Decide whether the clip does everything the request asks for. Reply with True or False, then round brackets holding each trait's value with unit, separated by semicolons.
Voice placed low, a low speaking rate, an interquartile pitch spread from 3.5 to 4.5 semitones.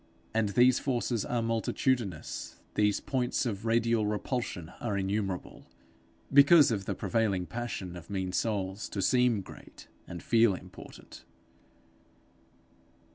True (110 Hz; 120 wpm; 3.8 semitones)